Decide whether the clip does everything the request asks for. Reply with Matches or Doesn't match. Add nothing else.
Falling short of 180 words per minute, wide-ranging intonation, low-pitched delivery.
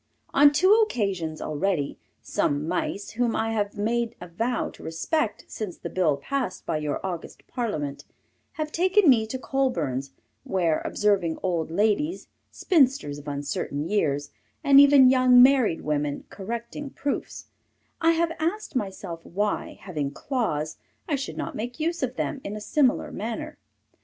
Doesn't match